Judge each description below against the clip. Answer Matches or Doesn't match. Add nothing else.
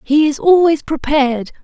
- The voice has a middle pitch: Doesn't match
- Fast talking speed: Doesn't match